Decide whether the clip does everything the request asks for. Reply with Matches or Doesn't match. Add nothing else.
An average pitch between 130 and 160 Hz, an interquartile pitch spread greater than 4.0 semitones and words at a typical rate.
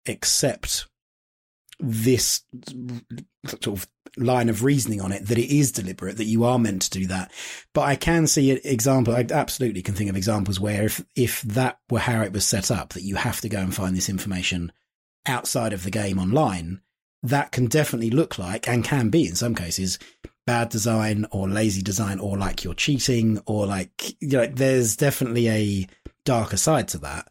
Doesn't match